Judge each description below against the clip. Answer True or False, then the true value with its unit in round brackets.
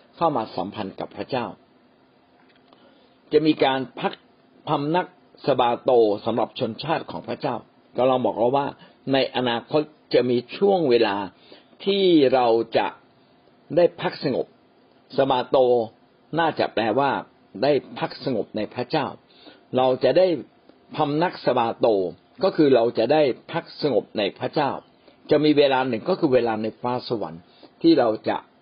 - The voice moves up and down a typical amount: True (4.9 semitones)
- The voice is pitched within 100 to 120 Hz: False (130 Hz)